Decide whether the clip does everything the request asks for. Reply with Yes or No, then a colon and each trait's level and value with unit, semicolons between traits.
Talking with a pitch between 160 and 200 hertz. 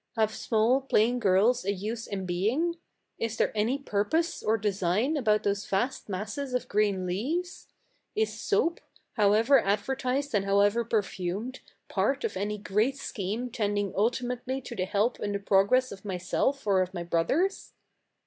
No: high, 215 Hz